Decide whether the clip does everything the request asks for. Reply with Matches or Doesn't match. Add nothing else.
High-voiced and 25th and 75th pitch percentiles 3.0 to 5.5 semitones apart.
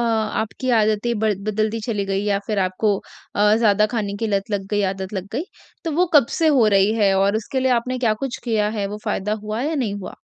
Doesn't match